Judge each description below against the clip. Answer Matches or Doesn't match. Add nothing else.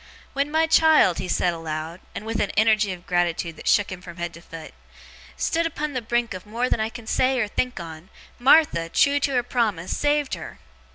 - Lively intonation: Matches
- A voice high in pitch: Matches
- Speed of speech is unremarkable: Doesn't match